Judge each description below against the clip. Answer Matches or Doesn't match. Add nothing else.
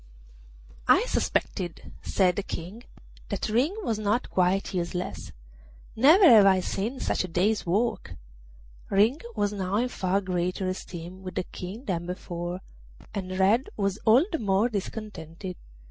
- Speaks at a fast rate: Doesn't match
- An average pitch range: Matches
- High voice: Matches